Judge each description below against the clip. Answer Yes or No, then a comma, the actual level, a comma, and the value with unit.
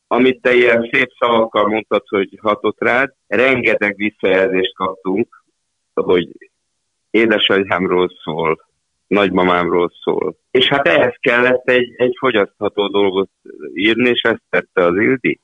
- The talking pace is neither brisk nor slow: Yes, average, 120 wpm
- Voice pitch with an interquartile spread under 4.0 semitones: No, average, 4.3 semitones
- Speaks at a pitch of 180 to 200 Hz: No, low, 105 Hz